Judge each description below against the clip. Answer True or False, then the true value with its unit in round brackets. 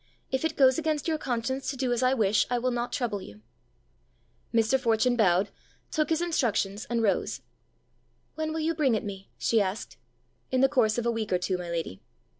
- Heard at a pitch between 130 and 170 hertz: False (240 Hz)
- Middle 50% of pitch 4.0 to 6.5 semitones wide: True (4.4 semitones)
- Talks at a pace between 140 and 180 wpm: False (205 wpm)